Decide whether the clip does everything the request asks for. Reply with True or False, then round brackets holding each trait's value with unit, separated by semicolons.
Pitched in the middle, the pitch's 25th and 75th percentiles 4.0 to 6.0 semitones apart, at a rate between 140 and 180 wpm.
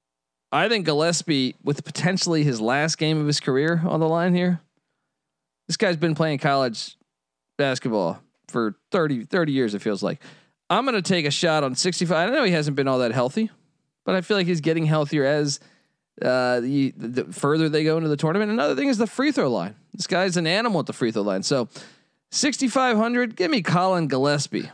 False (155 Hz; 4.8 semitones; 200 wpm)